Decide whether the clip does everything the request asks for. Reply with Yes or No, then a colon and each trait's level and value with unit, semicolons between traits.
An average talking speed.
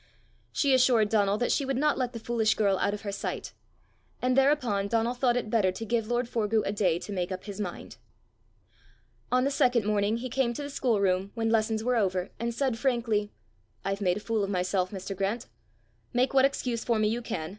No: fast, 215 wpm